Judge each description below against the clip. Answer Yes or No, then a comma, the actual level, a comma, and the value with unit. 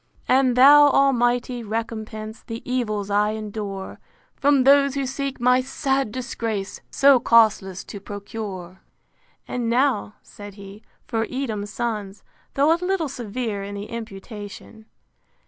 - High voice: Yes, high, 230 Hz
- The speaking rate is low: Yes, slow, 130 wpm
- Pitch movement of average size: Yes, average, 4.0 semitones